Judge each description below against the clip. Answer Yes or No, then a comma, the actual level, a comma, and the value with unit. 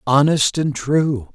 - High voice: No, medium, 140 Hz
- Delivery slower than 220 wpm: Yes, slow, 135 wpm